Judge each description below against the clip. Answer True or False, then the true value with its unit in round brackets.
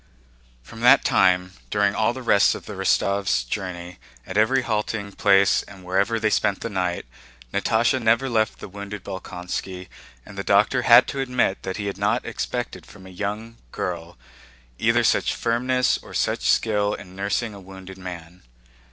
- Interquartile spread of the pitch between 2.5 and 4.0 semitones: True (3.2 semitones)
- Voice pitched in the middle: False (100 Hz)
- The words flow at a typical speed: True (170 wpm)